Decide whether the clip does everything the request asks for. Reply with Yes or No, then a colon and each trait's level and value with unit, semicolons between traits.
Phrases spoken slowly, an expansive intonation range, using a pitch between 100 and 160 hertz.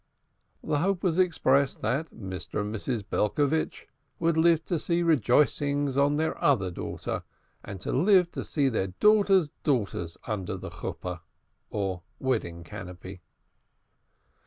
Yes: slow, 125 wpm; wide, 8.7 semitones; medium, 140 Hz